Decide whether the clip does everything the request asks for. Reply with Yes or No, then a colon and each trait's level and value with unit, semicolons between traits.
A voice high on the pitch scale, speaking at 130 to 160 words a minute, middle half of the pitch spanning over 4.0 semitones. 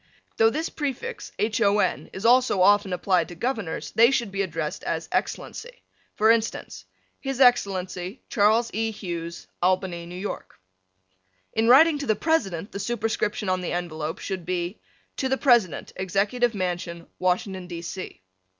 Yes: high, 200 Hz; average, 150 wpm; average, 4.6 semitones